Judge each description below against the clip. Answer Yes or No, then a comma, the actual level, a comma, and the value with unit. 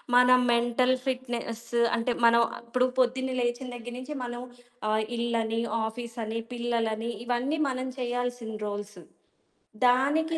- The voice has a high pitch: Yes, high, 240 Hz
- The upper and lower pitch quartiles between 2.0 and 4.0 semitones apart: No, narrow, 1.6 semitones